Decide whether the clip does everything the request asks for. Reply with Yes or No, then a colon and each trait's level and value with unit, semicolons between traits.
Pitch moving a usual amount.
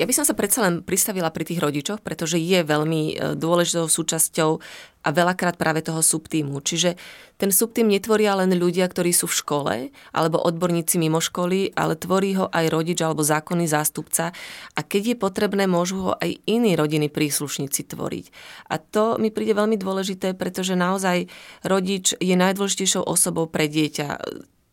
Yes: average, 3.1 semitones